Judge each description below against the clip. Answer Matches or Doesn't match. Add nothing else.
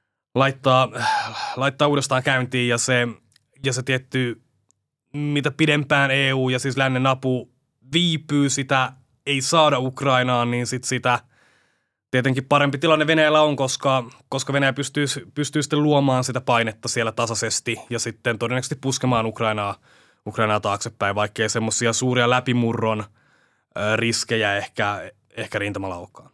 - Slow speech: Matches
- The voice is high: Doesn't match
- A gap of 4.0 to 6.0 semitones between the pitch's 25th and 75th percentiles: Doesn't match